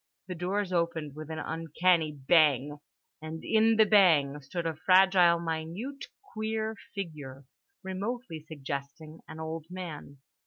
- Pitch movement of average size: Yes, average, 3.7 semitones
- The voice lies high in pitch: No, medium, 165 Hz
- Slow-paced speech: Yes, slow, 125 wpm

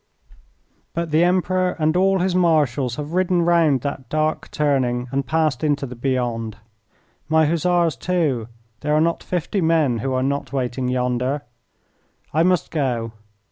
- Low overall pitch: No, medium, 150 Hz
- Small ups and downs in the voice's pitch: No, average, 4.7 semitones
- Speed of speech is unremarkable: Yes, average, 150 wpm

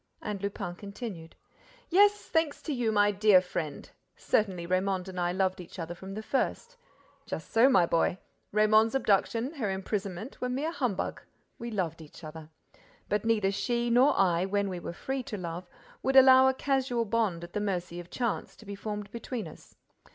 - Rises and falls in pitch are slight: No, average, 4.7 semitones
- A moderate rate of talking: Yes, average, 180 wpm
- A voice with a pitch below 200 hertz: No, high, 205 Hz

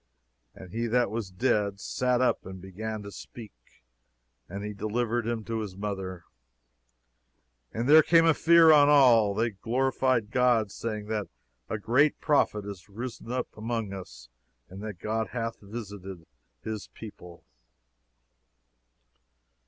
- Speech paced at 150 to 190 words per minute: No, average, 140 wpm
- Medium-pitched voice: No, low, 110 Hz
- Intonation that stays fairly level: No, average, 3.4 semitones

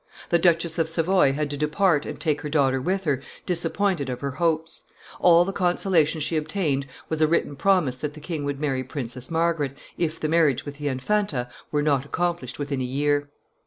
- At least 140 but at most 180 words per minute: No, average, 200 wpm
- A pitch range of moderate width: Yes, average, 3.2 semitones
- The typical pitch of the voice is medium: Yes, medium, 150 Hz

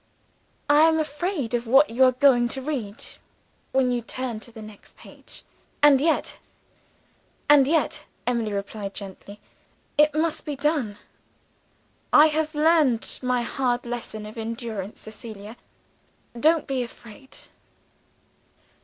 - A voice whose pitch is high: Yes, very high, 250 Hz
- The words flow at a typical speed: No, slow, 130 wpm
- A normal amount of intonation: Yes, average, 4.9 semitones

